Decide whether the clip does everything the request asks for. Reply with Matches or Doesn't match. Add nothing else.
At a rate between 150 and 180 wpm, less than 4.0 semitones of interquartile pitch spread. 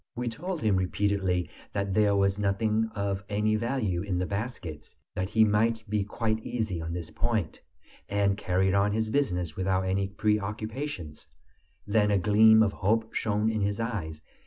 Matches